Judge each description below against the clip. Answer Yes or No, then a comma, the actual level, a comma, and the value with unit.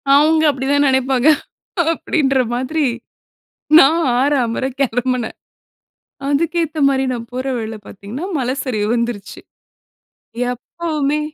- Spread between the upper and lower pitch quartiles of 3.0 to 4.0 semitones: Yes, average, 3.5 semitones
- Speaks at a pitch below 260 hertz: No, very high, 265 Hz